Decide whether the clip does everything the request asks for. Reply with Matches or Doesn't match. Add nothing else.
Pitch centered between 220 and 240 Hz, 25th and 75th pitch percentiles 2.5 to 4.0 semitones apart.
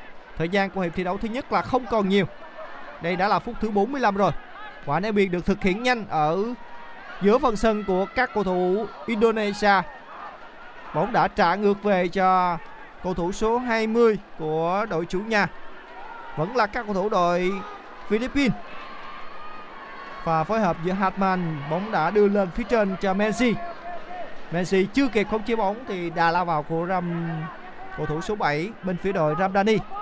Doesn't match